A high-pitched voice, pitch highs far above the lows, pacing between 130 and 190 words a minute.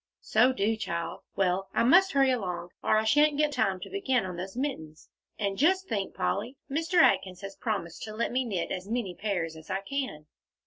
No: high, 215 Hz; wide, 6.3 semitones; fast, 205 wpm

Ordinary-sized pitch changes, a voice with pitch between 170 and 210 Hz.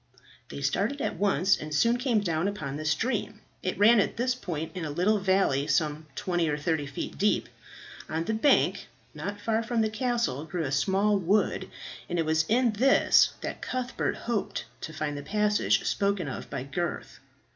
No: wide, 5.9 semitones; high, 190 Hz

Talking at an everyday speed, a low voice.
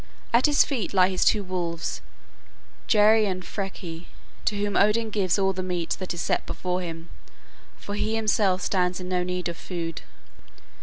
No: average, 170 wpm; medium, 185 Hz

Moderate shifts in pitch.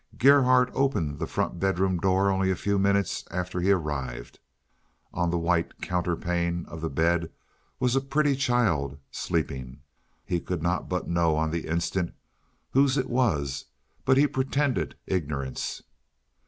No: wide, 6.9 semitones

